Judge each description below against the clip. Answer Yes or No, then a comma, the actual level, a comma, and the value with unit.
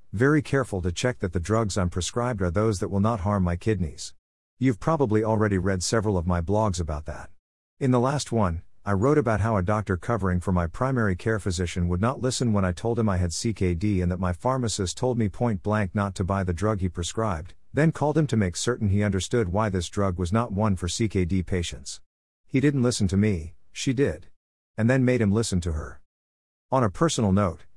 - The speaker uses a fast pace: Yes, fast, 225 wpm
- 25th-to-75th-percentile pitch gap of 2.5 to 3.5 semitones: No, average, 4.4 semitones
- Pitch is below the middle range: Yes, low, 100 Hz